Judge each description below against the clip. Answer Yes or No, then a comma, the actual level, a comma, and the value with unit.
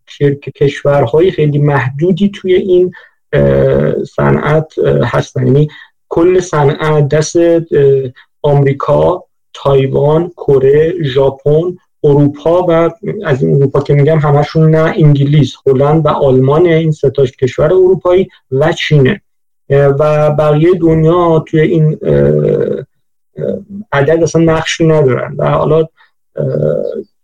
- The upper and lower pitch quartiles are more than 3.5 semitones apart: No, average, 2.9 semitones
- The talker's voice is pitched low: No, medium, 150 Hz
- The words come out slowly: Yes, slow, 100 wpm